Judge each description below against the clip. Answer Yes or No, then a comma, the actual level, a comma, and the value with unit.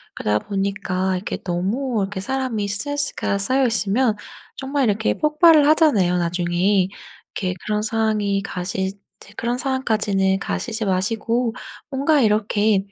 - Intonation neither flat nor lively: Yes, average, 4.9 semitones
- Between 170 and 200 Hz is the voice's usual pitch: No, high, 210 Hz